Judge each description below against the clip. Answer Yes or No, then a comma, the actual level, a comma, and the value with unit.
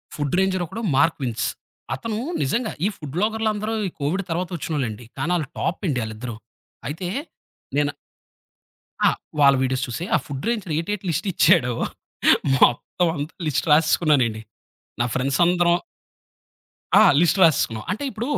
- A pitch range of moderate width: No, wide, 5.7 semitones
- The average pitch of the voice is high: No, medium, 160 Hz